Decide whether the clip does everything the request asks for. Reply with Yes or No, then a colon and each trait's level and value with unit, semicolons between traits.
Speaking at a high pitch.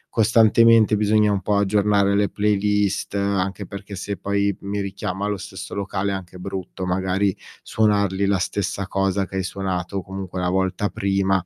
No: low, 100 Hz